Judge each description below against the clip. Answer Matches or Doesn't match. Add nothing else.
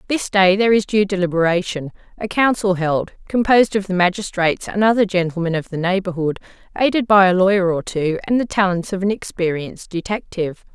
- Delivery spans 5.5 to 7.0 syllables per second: Matches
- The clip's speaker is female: Matches